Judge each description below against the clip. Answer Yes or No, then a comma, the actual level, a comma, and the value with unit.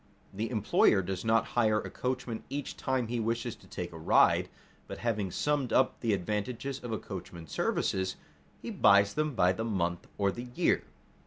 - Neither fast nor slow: Yes, average, 180 wpm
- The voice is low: Yes, low, 110 Hz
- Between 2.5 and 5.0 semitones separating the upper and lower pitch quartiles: Yes, average, 3.9 semitones